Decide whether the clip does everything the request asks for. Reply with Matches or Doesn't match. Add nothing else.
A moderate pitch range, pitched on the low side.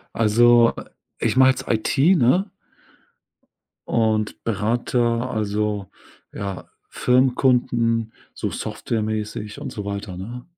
Doesn't match